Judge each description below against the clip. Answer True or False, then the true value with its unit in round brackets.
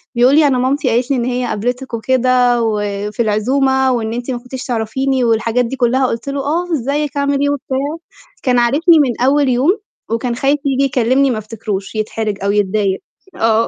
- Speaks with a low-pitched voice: False (250 Hz)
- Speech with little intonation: False (3.1 semitones)